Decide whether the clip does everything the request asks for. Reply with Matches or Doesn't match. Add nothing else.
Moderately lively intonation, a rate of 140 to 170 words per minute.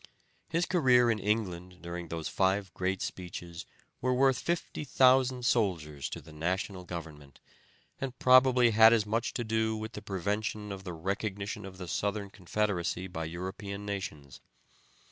Matches